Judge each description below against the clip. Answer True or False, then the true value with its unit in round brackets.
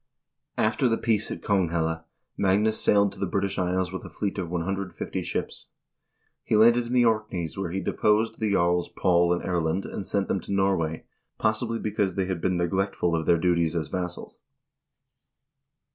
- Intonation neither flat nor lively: True (3.3 semitones)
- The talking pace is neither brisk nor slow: True (175 wpm)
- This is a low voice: True (95 Hz)